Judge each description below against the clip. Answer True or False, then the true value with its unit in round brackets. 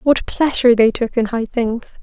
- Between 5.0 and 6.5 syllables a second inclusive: False (4.8 syllables/s)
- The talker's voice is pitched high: True (240 Hz)